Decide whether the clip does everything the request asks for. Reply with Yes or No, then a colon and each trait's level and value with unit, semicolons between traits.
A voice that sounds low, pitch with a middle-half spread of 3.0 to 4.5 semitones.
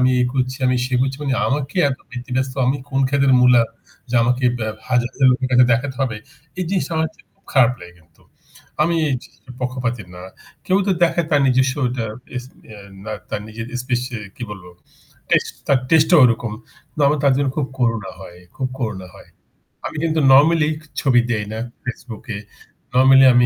No: low, 130 Hz; narrow, 2.6 semitones